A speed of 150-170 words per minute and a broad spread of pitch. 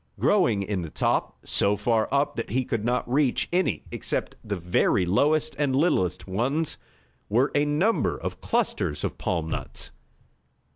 Yes: average, 155 wpm; wide, 6.9 semitones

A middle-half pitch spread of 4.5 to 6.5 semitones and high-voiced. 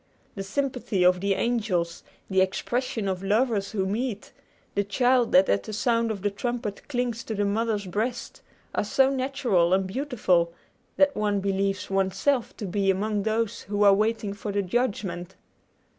No: average, 3.6 semitones; high, 205 Hz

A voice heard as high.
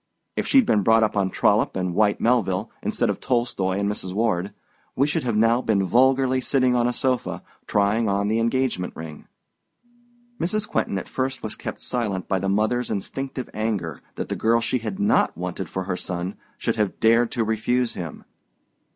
No: low, 110 Hz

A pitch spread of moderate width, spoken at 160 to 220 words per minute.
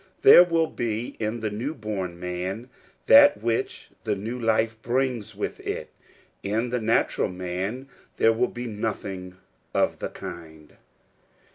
No: average, 3.7 semitones; average, 145 wpm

